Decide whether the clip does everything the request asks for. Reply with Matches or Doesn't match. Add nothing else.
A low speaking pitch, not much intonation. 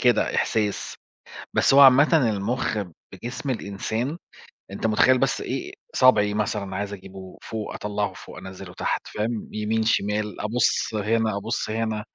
Matches